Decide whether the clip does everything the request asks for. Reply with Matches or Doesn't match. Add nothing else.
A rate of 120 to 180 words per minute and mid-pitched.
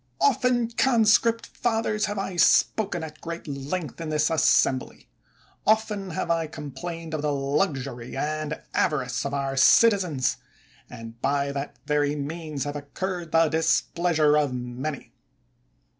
Matches